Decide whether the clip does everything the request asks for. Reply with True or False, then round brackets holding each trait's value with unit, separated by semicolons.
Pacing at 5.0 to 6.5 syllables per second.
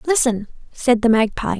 False (4.8 syllables/s)